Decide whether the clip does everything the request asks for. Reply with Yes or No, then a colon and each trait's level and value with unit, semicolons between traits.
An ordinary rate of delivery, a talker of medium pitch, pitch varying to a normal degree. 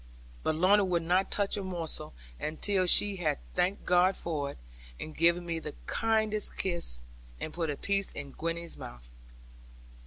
Yes: average, 160 wpm; medium, 175 Hz; average, 3.6 semitones